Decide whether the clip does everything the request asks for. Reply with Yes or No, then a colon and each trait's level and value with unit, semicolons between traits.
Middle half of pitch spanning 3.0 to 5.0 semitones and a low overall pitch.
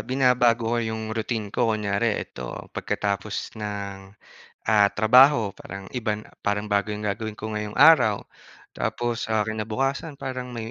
No: narrow, 2.5 semitones; low, 110 Hz